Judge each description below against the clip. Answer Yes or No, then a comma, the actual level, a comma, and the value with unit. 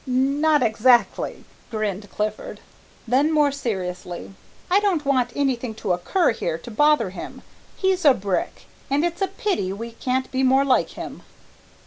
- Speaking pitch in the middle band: No, very high, 255 Hz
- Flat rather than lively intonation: No, wide, 5.6 semitones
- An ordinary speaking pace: Yes, average, 150 wpm